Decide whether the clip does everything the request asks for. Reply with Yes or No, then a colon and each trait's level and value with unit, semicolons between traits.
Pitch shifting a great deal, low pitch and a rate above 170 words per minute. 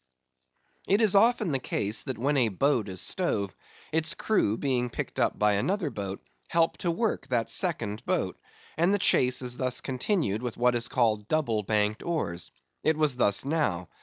Yes: wide, 7.3 semitones; low, 125 Hz; average, 180 wpm